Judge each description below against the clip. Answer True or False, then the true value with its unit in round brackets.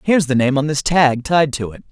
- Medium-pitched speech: True (145 Hz)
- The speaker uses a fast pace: True (280 wpm)